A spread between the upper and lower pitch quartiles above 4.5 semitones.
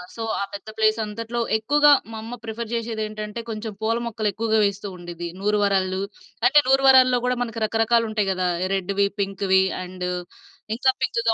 No: narrow, 2.6 semitones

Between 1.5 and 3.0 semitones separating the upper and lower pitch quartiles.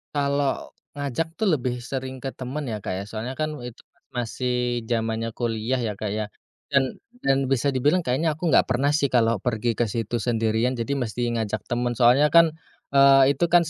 No: average, 3.4 semitones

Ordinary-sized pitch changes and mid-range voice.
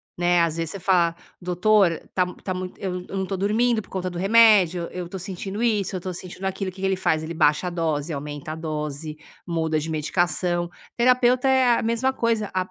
Yes: average, 3.5 semitones; medium, 180 Hz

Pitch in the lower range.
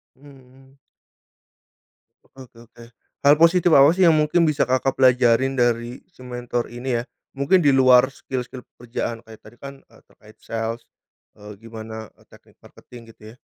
Yes: low, 125 Hz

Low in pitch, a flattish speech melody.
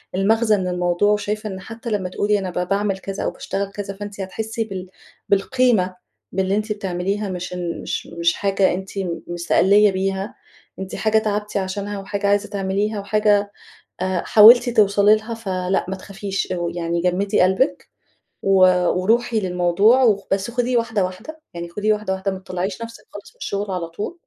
No: high, 200 Hz; narrow, 2.2 semitones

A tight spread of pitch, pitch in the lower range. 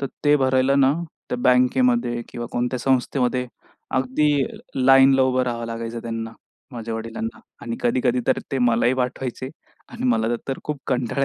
Yes: narrow, 2.0 semitones; low, 125 Hz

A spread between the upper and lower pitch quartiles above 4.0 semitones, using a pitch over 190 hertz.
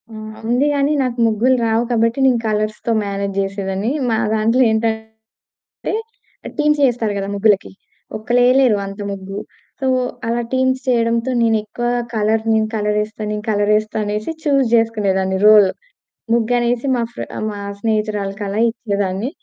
No: narrow, 2.4 semitones; high, 220 Hz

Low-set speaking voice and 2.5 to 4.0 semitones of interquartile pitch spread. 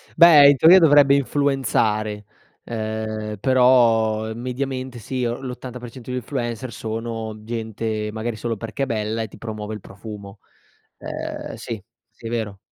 Yes: low, 115 Hz; average, 2.8 semitones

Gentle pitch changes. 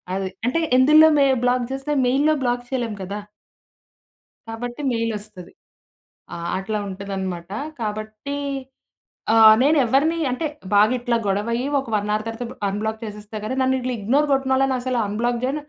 No: average, 3.8 semitones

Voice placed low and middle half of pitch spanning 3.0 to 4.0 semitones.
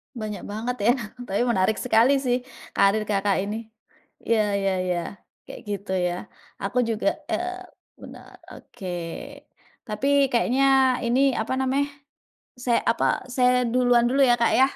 No: high, 240 Hz; average, 3.7 semitones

